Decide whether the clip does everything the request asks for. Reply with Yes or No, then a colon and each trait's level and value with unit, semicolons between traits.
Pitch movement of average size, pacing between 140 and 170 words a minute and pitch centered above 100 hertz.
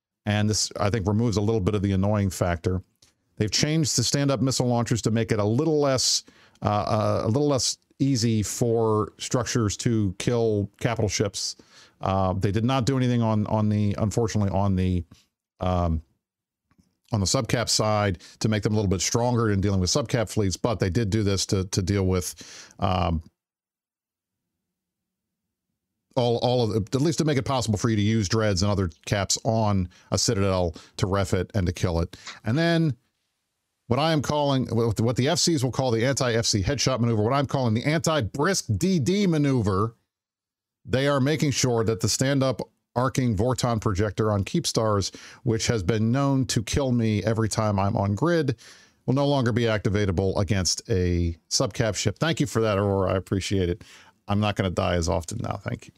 No: average, 3.9 semitones; average, 190 wpm; low, 110 Hz